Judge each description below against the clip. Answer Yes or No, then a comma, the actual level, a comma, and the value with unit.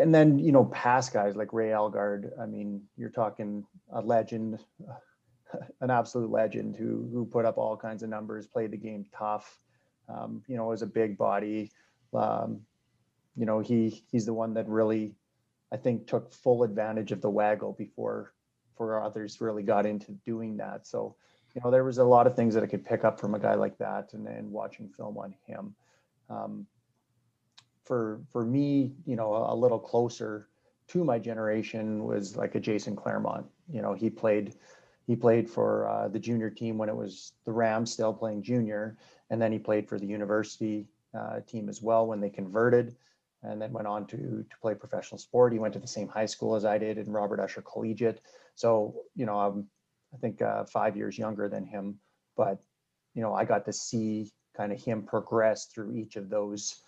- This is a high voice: No, low, 110 Hz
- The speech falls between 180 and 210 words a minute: Yes, average, 200 wpm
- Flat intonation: Yes, narrow, 1.7 semitones